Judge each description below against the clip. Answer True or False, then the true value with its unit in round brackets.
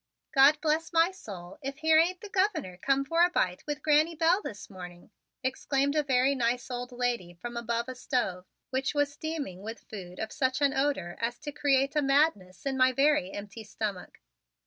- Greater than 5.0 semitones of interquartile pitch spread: True (5.5 semitones)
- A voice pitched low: False (265 Hz)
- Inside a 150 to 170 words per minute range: False (195 wpm)